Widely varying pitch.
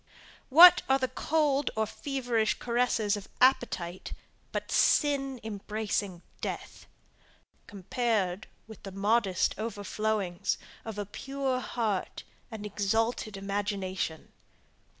No: average, 3.9 semitones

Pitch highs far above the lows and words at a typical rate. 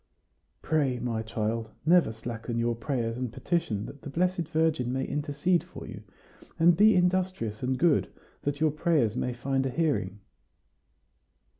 Yes: wide, 5.9 semitones; average, 150 wpm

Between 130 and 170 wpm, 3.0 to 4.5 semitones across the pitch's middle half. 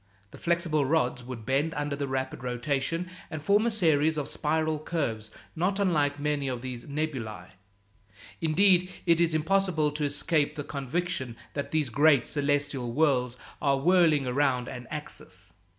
Yes: average, 150 wpm; average, 3.4 semitones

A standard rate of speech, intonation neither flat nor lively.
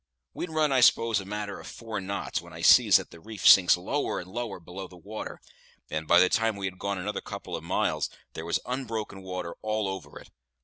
No: fast, 230 wpm; average, 3.4 semitones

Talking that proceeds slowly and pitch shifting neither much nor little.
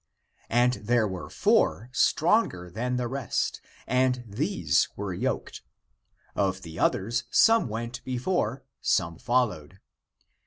Yes: slow, 115 wpm; average, 4.7 semitones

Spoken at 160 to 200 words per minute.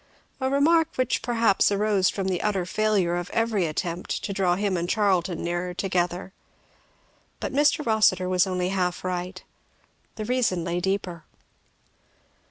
No: average, 145 wpm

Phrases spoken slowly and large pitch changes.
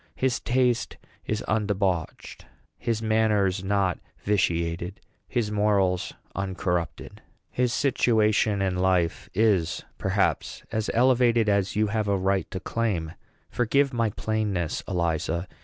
No: slow, 115 wpm; average, 3.2 semitones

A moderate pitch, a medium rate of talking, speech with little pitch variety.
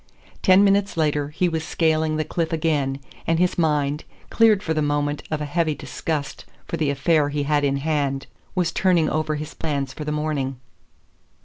Yes: medium, 155 Hz; average, 185 wpm; narrow, 2.2 semitones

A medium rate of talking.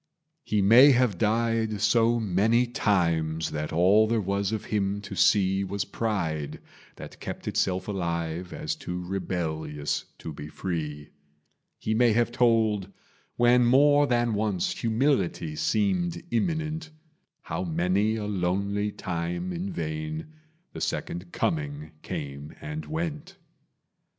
No: slow, 125 wpm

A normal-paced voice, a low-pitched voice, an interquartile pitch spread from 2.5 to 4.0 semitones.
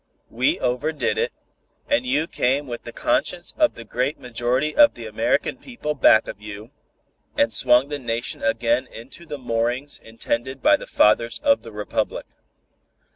No: average, 160 wpm; low, 130 Hz; average, 4.9 semitones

